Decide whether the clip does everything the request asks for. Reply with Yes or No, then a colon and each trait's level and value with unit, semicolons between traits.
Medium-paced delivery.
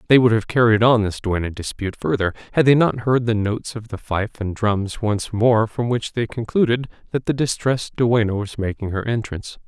No: fast, 210 wpm